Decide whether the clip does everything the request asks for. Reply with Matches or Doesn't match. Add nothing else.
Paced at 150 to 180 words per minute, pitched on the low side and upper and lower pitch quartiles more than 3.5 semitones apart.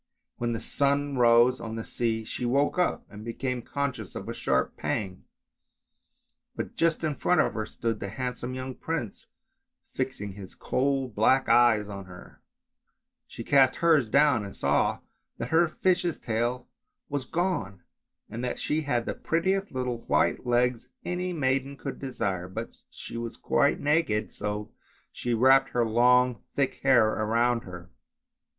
Matches